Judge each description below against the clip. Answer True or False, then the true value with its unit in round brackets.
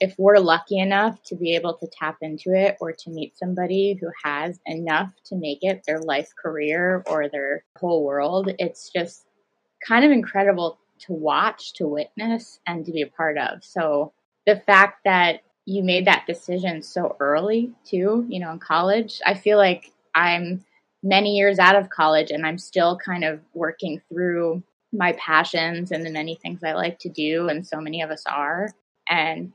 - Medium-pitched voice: True (175 Hz)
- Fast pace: False (185 wpm)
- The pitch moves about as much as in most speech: True (3.5 semitones)